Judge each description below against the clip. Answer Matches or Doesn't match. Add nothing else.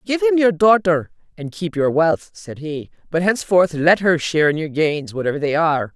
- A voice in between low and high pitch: Matches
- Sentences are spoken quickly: Matches